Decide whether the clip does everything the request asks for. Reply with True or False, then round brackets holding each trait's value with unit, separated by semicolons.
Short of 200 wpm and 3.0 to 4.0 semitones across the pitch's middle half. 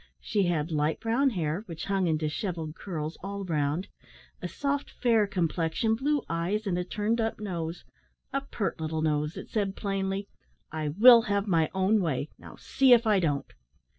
False (175 wpm; 5.2 semitones)